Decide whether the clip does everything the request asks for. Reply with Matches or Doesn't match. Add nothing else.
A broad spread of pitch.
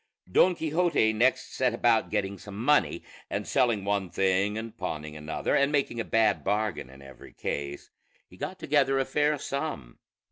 Matches